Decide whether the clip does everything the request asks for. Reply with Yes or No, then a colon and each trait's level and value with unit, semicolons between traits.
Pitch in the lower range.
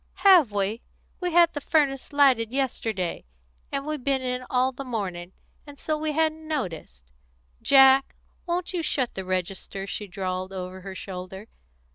No: very high, 255 Hz